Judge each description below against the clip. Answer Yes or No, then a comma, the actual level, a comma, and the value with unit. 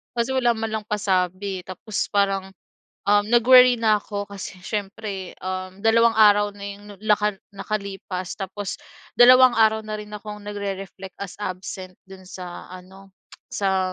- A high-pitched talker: Yes, high, 200 Hz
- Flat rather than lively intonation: Yes, narrow, 2.2 semitones